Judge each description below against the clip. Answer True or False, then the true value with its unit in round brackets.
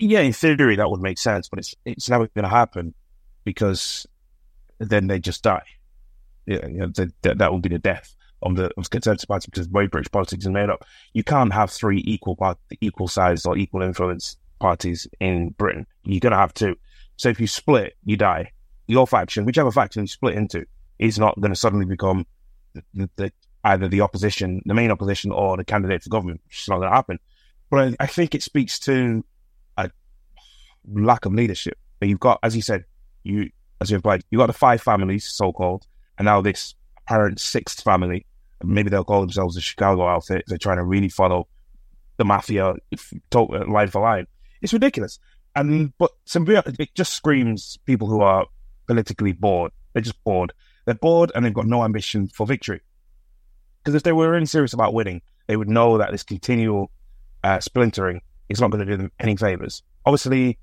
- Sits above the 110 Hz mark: False (100 Hz)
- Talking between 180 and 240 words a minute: True (200 wpm)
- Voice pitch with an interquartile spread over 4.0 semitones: False (3.7 semitones)